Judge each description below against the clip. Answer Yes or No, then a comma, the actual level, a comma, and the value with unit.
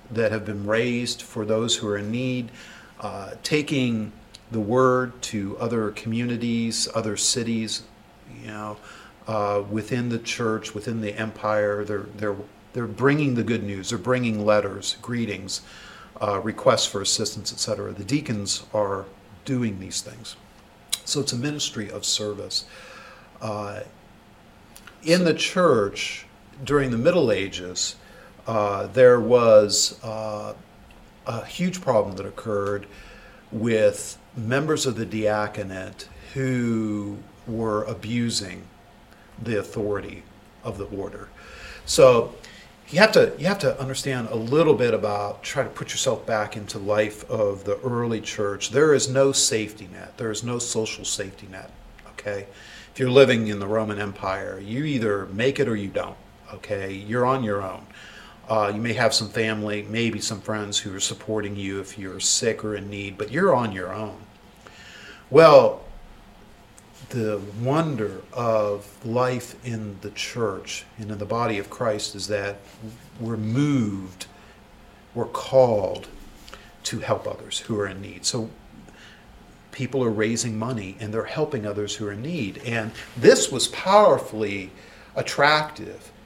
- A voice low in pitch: Yes, low, 110 Hz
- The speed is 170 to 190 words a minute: No, average, 145 wpm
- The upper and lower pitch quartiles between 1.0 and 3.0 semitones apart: Yes, narrow, 2.6 semitones